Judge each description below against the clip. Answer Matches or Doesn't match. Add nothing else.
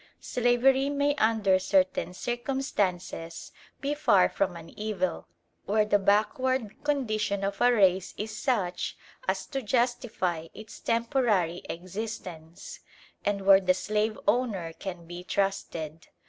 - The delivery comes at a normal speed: Doesn't match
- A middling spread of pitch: Matches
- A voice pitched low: Doesn't match